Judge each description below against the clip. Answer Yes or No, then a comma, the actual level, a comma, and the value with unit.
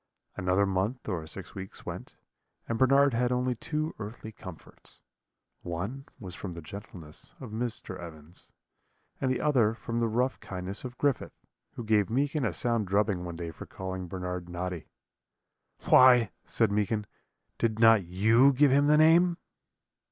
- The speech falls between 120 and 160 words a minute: Yes, average, 155 wpm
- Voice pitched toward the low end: Yes, low, 110 Hz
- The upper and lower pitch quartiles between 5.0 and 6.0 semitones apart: Yes, wide, 5.5 semitones